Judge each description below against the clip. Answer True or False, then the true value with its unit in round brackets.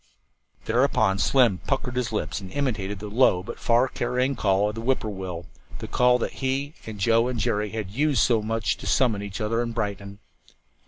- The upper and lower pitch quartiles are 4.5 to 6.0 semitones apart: False (3.8 semitones)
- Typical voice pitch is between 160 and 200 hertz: False (115 Hz)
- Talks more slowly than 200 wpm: False (205 wpm)